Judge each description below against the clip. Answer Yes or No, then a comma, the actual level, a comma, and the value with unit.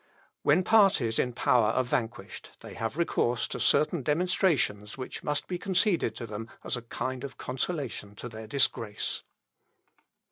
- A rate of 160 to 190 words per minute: No, average, 150 wpm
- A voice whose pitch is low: Yes, low, 125 Hz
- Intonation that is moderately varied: No, wide, 5.9 semitones